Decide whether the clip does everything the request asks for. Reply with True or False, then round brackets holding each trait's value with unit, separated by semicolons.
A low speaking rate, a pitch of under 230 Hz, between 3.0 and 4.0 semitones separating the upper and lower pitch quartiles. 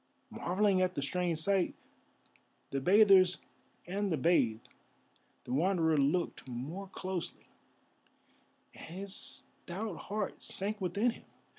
True (115 wpm; 185 Hz; 3.5 semitones)